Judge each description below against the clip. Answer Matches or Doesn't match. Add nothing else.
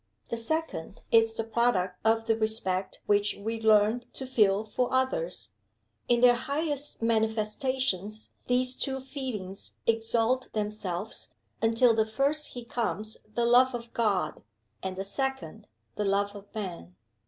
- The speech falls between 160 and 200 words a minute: Doesn't match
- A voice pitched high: Matches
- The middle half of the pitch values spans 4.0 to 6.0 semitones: Doesn't match